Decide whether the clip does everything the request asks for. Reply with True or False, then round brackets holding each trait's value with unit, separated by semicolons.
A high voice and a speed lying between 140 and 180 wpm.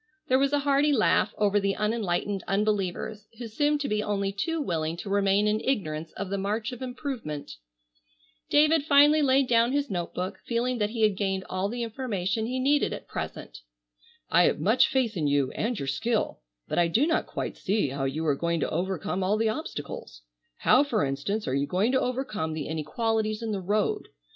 False (210 Hz; 200 wpm)